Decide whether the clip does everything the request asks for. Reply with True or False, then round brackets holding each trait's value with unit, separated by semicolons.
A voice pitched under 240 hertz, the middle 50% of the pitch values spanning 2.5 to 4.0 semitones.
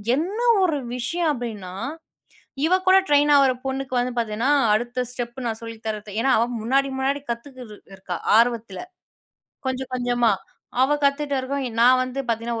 False (250 Hz; 3.1 semitones)